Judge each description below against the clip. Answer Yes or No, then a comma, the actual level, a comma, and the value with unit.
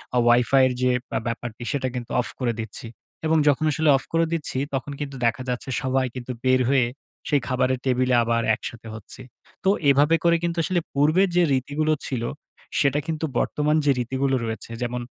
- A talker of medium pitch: No, low, 130 Hz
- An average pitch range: Yes, average, 3.2 semitones